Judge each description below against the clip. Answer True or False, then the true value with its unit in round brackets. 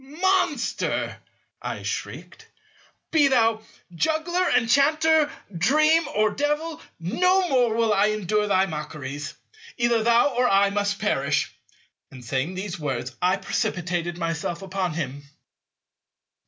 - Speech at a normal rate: False (115 wpm)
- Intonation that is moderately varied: False (8.8 semitones)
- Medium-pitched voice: False (210 Hz)